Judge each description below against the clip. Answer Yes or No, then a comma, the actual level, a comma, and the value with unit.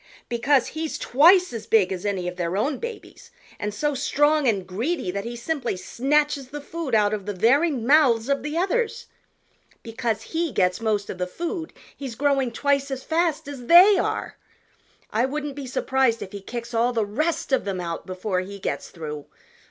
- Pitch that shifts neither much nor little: No, wide, 6.3 semitones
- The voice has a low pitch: No, very high, 250 Hz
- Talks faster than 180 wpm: Yes, average, 190 wpm